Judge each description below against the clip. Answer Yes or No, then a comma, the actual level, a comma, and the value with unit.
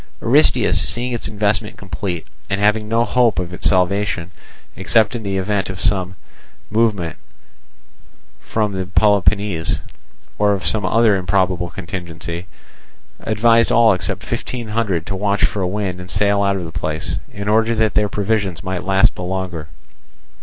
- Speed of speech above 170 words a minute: No, average, 155 wpm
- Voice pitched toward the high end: No, low, 100 Hz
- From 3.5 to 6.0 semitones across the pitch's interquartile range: No, average, 2.7 semitones